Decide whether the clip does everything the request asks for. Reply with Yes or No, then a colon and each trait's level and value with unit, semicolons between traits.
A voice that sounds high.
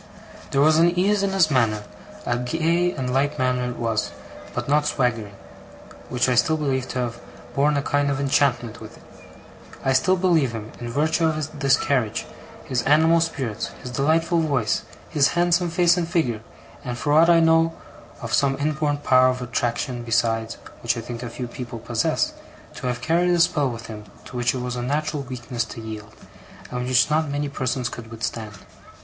No: low, 135 Hz